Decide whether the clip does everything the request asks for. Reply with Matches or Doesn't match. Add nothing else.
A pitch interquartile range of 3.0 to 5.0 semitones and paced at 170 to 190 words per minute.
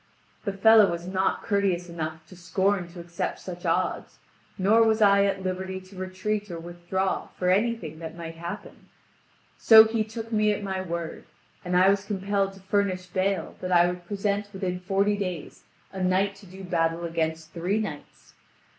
Doesn't match